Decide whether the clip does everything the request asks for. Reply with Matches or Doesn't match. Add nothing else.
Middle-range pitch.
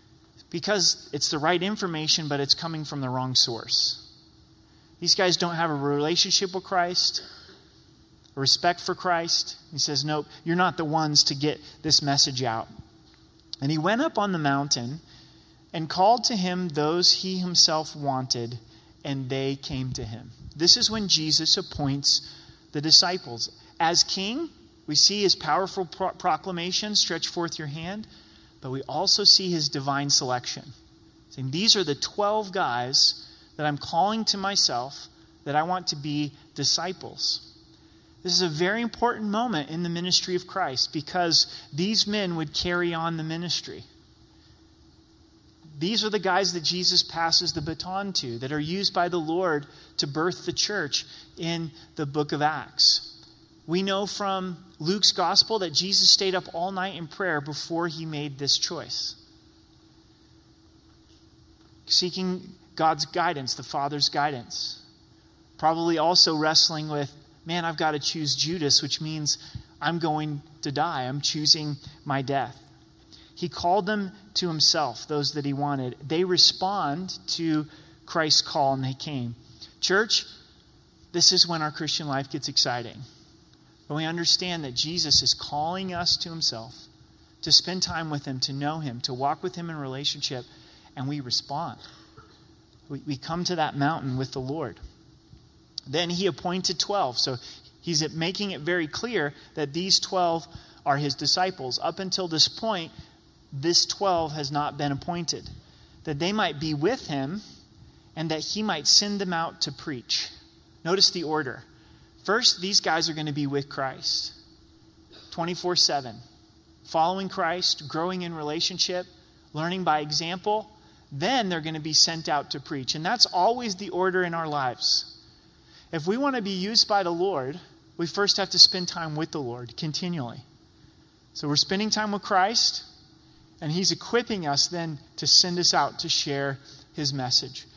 Matches